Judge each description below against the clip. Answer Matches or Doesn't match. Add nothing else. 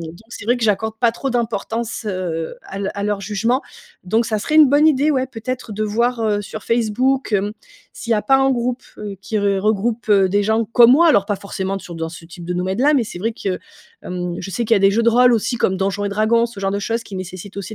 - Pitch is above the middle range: Matches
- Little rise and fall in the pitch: Doesn't match